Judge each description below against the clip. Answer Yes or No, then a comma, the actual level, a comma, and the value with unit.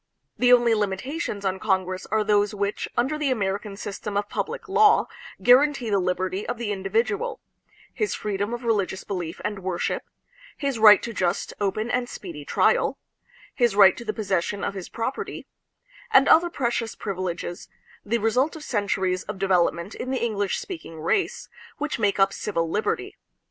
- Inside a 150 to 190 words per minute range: Yes, average, 170 wpm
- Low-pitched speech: No, high, 210 Hz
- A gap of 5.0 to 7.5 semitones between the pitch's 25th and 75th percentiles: No, average, 4.1 semitones